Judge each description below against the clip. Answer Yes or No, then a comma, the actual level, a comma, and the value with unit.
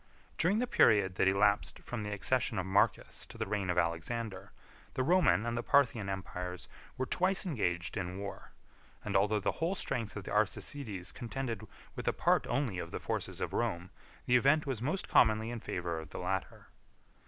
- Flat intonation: No, wide, 5.5 semitones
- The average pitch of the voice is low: Yes, low, 105 Hz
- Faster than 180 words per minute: Yes, average, 190 wpm